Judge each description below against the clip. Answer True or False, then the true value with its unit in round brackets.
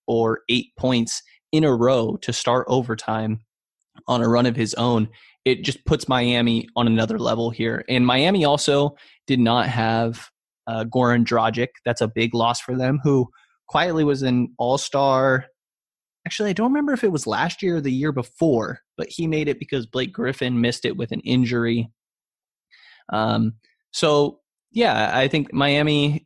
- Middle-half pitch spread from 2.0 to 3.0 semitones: False (3.7 semitones)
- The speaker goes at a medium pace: True (170 wpm)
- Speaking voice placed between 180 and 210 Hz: False (125 Hz)